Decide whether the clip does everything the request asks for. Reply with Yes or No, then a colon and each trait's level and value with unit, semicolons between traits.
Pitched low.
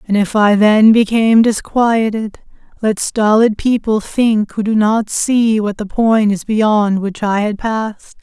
No: high, 215 Hz